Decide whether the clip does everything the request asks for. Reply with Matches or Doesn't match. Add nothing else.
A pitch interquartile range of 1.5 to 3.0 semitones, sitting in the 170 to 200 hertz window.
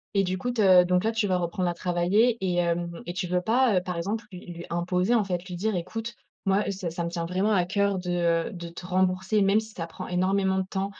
Matches